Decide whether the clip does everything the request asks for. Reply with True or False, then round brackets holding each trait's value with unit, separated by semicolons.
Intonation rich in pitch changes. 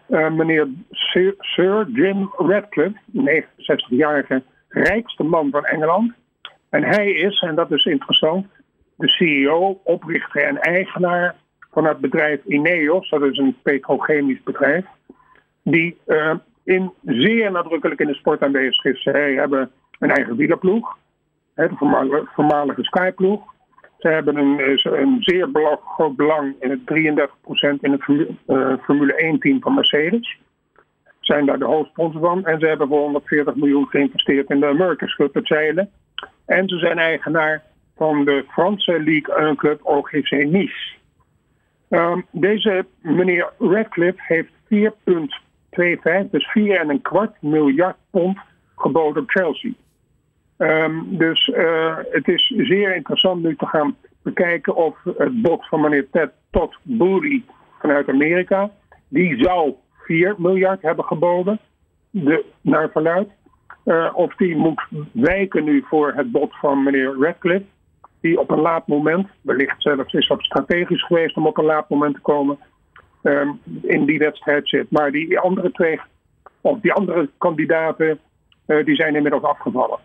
False (4.2 semitones)